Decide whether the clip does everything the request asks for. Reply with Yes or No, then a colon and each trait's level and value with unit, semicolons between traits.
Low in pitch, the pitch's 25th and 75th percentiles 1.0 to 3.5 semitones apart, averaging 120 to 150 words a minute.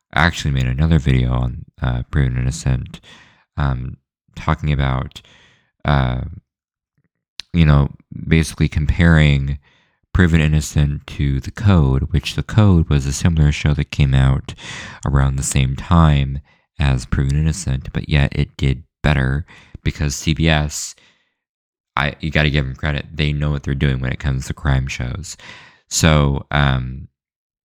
Yes: very low, 70 Hz; narrow, 2.4 semitones; average, 140 wpm